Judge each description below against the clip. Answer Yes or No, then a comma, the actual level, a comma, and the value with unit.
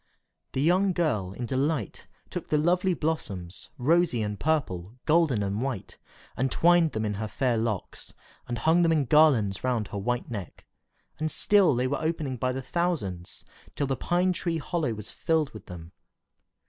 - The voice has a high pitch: No, low, 130 Hz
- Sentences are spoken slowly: No, average, 170 wpm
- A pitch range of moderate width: No, wide, 7.1 semitones